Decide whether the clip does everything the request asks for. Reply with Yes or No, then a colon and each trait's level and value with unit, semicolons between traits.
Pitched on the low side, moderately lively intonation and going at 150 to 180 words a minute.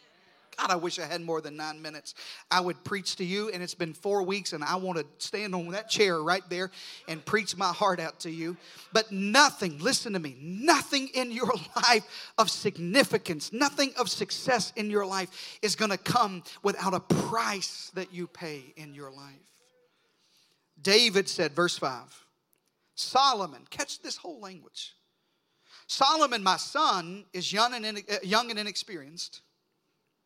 No: high, 190 Hz; average, 4.1 semitones; average, 165 wpm